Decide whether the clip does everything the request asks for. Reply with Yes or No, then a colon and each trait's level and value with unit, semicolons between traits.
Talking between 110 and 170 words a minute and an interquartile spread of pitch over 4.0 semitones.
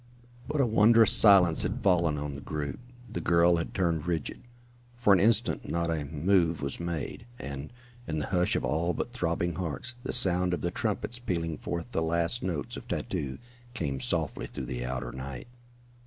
No: average, 185 wpm; average, 4.5 semitones